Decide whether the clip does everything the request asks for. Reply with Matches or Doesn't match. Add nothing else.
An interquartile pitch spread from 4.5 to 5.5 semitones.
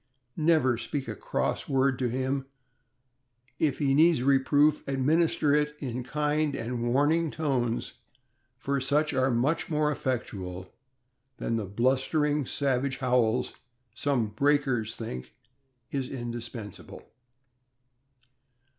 Doesn't match